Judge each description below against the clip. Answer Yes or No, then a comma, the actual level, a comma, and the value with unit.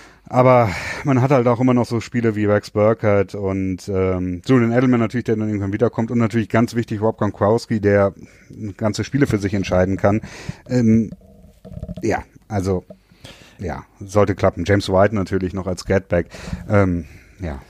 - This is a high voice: No, low, 105 Hz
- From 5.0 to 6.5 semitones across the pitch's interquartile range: No, average, 3.4 semitones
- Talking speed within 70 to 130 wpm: No, average, 165 wpm